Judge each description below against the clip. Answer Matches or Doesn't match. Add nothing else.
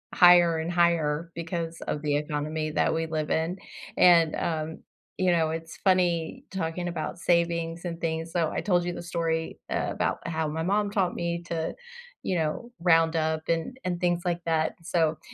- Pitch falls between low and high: Matches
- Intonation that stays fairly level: Matches